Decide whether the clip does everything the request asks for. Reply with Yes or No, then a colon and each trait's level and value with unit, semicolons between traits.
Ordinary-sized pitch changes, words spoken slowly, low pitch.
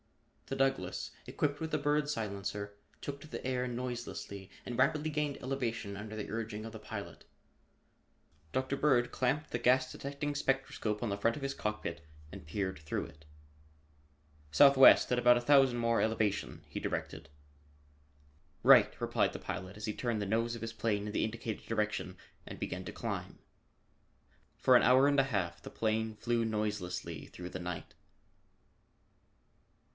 No: average, 4.3 semitones; average, 160 wpm; low, 115 Hz